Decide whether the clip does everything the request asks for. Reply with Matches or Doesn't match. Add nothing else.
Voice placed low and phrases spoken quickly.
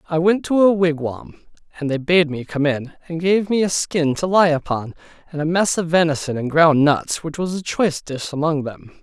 Doesn't match